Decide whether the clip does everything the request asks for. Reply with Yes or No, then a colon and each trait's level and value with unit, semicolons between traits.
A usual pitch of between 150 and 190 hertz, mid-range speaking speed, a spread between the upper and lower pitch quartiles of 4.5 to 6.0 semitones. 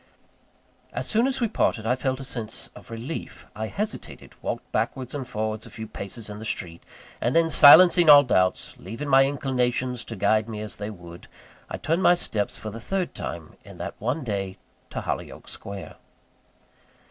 No: low, 120 Hz; average, 180 wpm; average, 5.1 semitones